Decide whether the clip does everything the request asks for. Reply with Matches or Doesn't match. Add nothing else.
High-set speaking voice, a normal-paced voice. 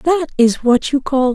Doesn't match